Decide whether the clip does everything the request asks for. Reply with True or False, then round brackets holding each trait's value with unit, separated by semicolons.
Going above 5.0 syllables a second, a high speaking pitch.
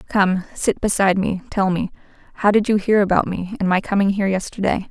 True (5.9 syllables/s; 195 Hz)